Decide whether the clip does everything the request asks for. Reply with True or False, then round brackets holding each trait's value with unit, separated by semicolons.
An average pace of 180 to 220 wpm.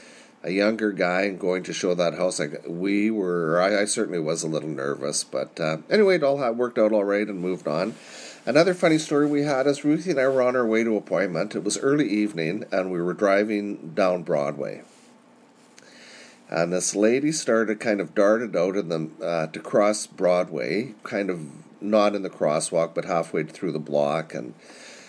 True (195 wpm)